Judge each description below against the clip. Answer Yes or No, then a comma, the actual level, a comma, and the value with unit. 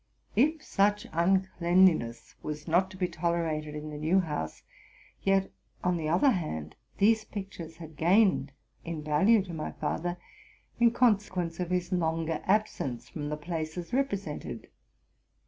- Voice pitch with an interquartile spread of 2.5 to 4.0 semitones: Yes, average, 3.7 semitones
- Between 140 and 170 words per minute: Yes, average, 145 wpm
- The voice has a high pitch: No, medium, 175 Hz